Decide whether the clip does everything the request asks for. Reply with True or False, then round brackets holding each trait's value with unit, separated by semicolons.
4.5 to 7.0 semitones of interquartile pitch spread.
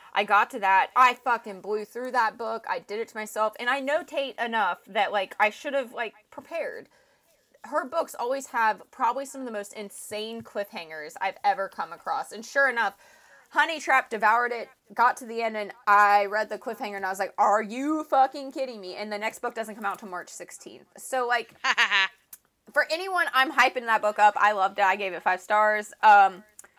False (4.1 semitones)